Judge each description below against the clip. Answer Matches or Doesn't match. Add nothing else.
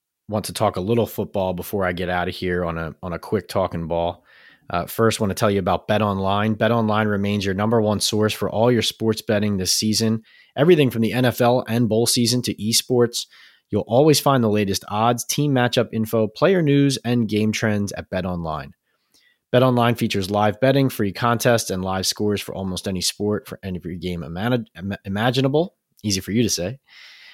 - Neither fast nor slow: Doesn't match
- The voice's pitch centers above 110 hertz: Doesn't match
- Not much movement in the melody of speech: Doesn't match